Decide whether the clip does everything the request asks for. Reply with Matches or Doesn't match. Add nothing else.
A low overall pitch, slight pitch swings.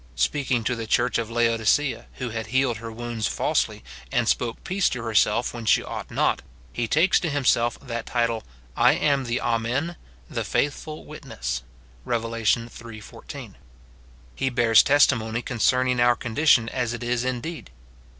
Matches